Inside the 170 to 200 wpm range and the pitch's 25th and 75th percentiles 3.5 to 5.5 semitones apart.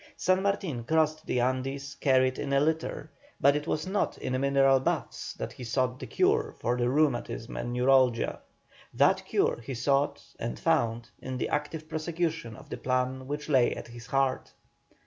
No: average, 175 wpm; average, 3.1 semitones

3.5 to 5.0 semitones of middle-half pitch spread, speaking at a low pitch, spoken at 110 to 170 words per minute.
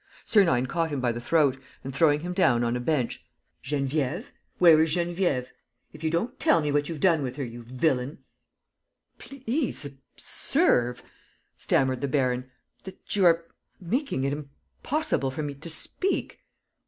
No: average, 4.7 semitones; medium, 145 Hz; average, 160 wpm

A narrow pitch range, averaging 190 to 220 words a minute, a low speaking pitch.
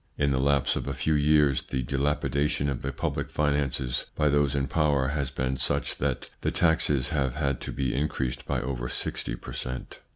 Yes: narrow, 1.9 semitones; average, 195 wpm; very low, 70 Hz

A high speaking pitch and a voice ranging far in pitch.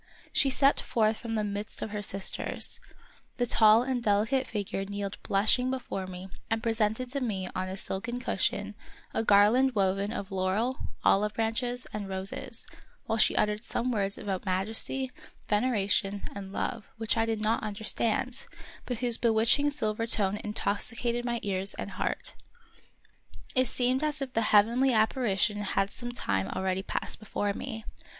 No: high, 220 Hz; average, 3.3 semitones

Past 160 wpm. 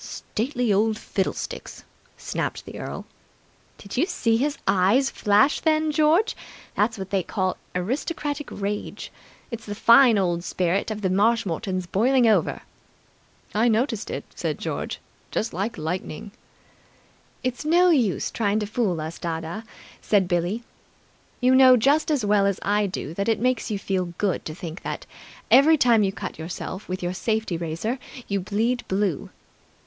No: average, 155 wpm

